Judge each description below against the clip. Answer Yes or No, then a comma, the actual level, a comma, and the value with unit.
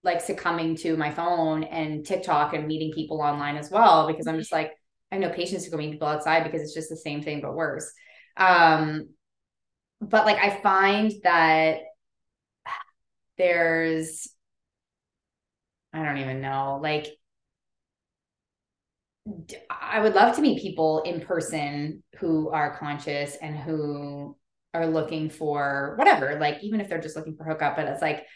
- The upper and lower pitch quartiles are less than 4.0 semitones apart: Yes, average, 2.9 semitones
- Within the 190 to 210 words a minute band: No, average, 155 wpm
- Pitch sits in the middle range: Yes, medium, 160 Hz